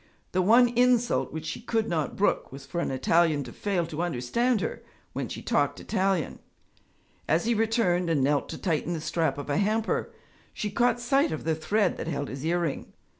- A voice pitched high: No, medium, 175 Hz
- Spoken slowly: No, average, 195 wpm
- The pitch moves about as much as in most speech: No, wide, 6.1 semitones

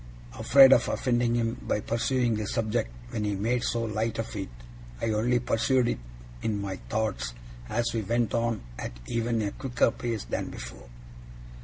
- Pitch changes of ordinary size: No, narrow, 2.0 semitones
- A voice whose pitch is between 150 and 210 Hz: No, low, 115 Hz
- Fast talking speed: No, average, 170 wpm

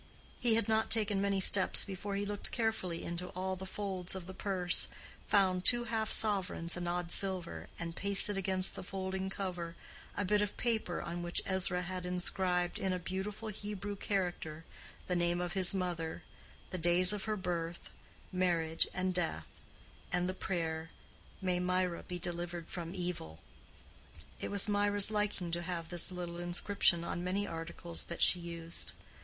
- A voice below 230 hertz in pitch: Yes, medium, 185 Hz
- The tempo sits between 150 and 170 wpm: Yes, average, 165 wpm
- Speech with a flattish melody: Yes, narrow, 2.3 semitones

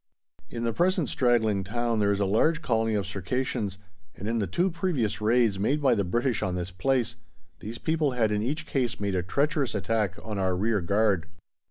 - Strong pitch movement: No, average, 4.2 semitones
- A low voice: Yes, low, 110 Hz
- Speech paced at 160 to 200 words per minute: Yes, average, 195 wpm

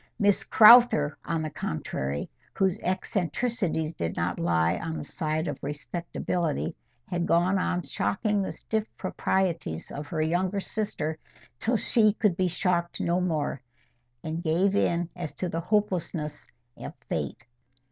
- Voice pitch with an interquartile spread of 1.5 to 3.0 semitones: No, average, 3.6 semitones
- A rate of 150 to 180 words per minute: No, average, 140 wpm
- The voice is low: No, medium, 170 Hz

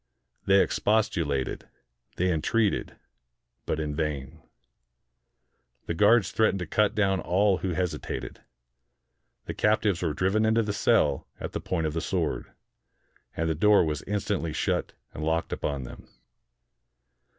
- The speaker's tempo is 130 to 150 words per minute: Yes, slow, 135 wpm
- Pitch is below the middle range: Yes, very low, 90 Hz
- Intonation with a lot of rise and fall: No, average, 4.8 semitones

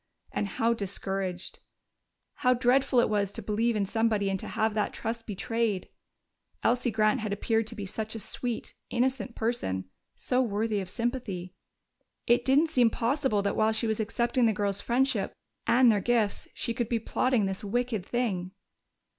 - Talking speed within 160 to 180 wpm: Yes, average, 170 wpm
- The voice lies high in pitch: Yes, high, 225 Hz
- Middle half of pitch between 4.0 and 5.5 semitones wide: No, average, 3.0 semitones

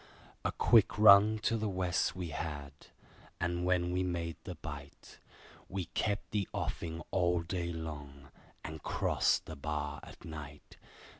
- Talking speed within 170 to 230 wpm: No, average, 145 wpm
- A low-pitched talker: Yes, very low, 85 Hz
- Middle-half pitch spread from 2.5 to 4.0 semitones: Yes, average, 3.2 semitones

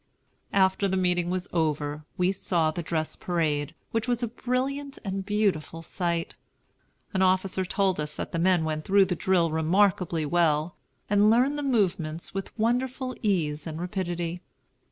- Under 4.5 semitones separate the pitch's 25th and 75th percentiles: Yes, average, 3.9 semitones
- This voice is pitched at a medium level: Yes, medium, 180 Hz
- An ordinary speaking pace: Yes, average, 155 wpm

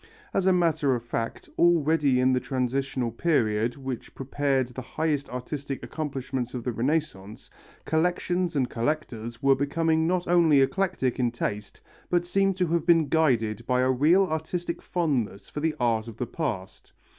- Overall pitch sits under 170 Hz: Yes, medium, 140 Hz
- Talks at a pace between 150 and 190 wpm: Yes, average, 160 wpm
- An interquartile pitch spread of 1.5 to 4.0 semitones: No, average, 4.8 semitones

